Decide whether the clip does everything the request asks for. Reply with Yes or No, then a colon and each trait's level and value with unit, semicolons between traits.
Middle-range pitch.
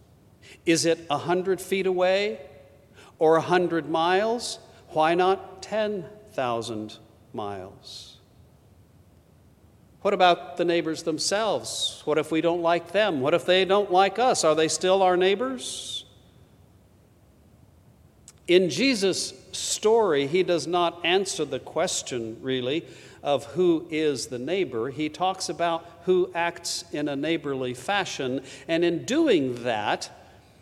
Yes: medium, 165 Hz